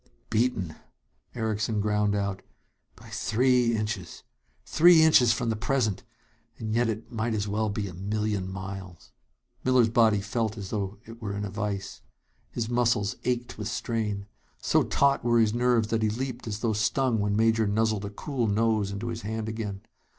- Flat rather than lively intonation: Yes, narrow, 2.2 semitones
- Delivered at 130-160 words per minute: No, average, 170 wpm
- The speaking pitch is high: No, low, 110 Hz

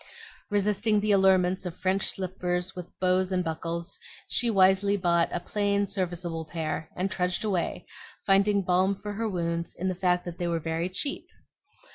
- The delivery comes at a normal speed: Yes, average, 165 wpm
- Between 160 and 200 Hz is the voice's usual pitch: Yes, medium, 185 Hz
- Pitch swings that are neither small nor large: No, narrow, 2.3 semitones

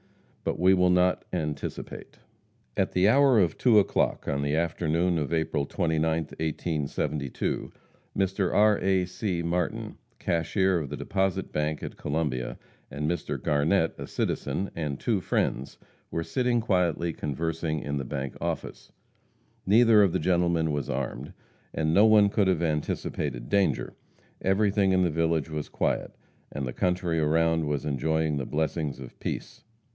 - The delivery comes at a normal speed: Yes, average, 150 wpm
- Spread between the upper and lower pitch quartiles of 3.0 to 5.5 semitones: Yes, average, 3.9 semitones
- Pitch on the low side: Yes, very low, 80 Hz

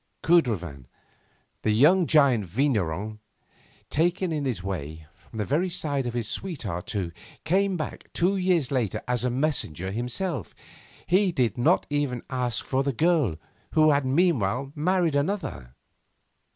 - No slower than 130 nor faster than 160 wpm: Yes, average, 140 wpm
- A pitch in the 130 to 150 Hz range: Yes, low, 135 Hz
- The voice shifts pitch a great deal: Yes, wide, 7.4 semitones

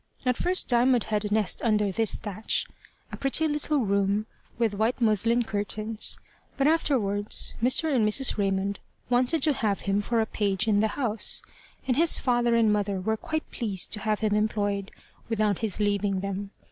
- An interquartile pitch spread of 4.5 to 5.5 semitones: No, average, 3.0 semitones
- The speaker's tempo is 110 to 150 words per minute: No, average, 175 wpm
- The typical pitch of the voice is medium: No, high, 215 Hz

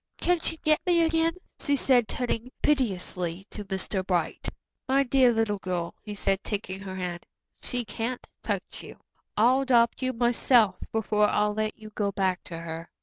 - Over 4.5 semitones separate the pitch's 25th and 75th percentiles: Yes, average, 5.0 semitones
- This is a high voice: Yes, high, 215 Hz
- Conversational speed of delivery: Yes, average, 170 wpm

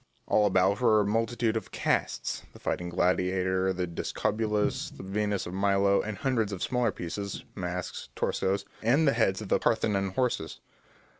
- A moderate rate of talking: Yes, average, 160 wpm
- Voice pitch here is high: No, low, 100 Hz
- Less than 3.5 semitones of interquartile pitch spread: Yes, average, 2.8 semitones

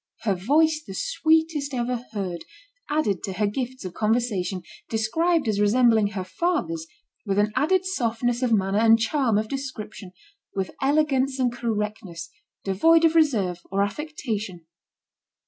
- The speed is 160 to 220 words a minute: No, average, 140 wpm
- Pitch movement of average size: No, wide, 6.0 semitones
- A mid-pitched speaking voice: No, high, 225 Hz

